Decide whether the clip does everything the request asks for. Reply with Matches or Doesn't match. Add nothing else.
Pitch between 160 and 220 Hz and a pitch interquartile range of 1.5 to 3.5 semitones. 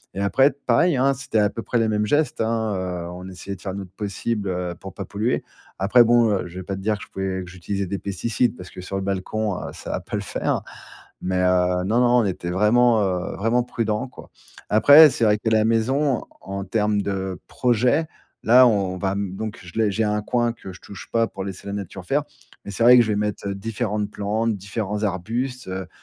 Doesn't match